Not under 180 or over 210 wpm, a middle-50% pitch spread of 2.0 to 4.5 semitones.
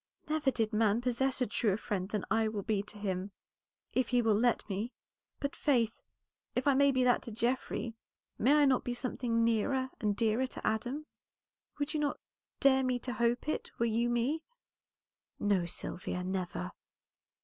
No: average, 170 wpm; average, 3.5 semitones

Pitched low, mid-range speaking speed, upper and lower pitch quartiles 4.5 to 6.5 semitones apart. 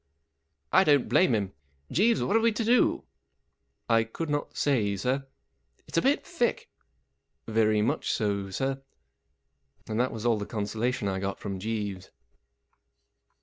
Yes: low, 115 Hz; average, 170 wpm; wide, 5.6 semitones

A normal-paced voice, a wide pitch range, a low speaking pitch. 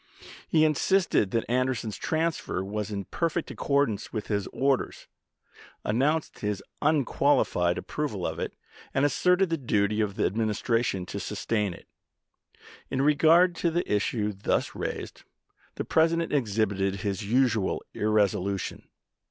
No: slow, 130 wpm; wide, 6.6 semitones; low, 115 Hz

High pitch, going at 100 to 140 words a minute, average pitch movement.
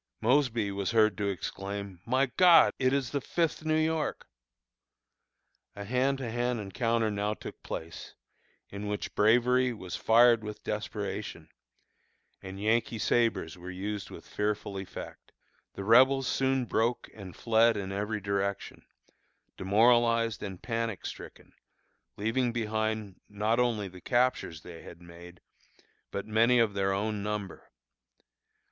No: low, 110 Hz; slow, 135 wpm; average, 3.3 semitones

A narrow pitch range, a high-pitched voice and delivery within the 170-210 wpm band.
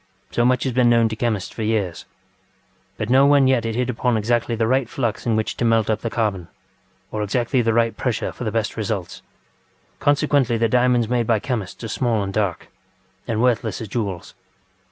No: narrow, 2.2 semitones; low, 115 Hz; average, 200 wpm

